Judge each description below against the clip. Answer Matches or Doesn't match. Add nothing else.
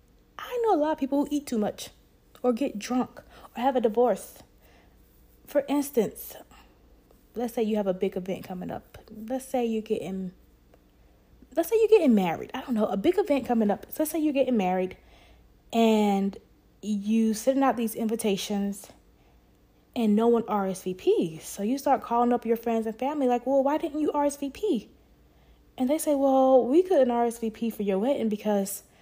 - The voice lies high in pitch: Matches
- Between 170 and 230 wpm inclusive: Matches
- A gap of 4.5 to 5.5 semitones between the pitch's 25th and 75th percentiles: Matches